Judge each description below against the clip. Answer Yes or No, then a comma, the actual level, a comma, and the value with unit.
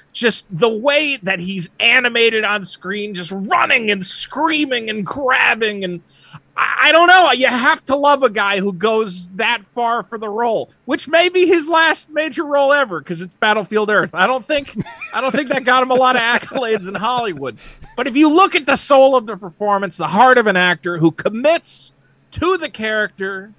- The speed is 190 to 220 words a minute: Yes, average, 200 wpm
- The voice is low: No, high, 235 Hz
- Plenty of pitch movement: Yes, wide, 5.9 semitones